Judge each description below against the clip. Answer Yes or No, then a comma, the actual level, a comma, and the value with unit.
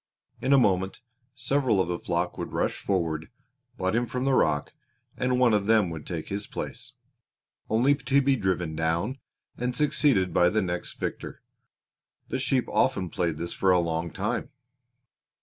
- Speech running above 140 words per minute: Yes, average, 165 wpm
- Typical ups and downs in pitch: No, wide, 6.6 semitones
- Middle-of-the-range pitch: No, low, 100 Hz